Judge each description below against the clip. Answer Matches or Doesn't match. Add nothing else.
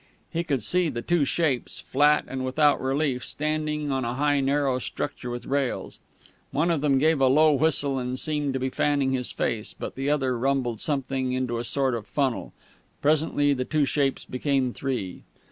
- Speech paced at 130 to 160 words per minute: Doesn't match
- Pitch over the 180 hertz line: Doesn't match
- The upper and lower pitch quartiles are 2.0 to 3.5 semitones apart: Matches